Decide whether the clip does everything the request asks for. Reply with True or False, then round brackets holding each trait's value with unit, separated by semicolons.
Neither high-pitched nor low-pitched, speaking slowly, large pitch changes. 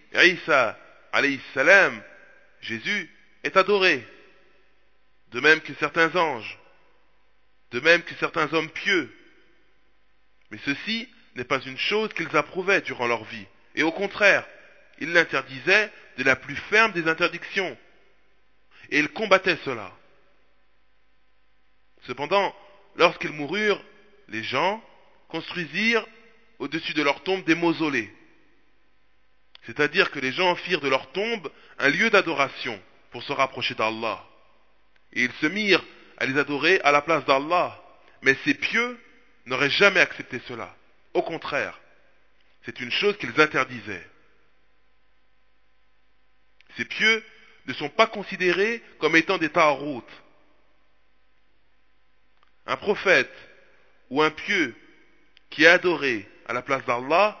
True (150 Hz; 120 wpm; 7.8 semitones)